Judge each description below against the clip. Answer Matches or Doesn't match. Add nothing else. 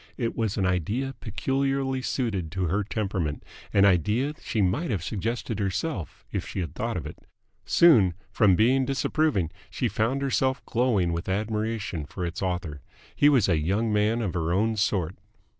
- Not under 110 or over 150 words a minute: Doesn't match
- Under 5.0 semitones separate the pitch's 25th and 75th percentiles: Doesn't match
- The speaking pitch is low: Matches